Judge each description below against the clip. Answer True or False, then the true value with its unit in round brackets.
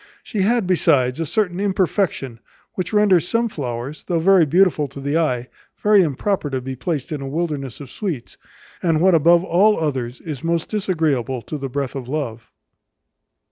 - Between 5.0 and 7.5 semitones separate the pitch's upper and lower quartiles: True (5.5 semitones)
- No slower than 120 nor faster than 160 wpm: False (175 wpm)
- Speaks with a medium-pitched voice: True (160 Hz)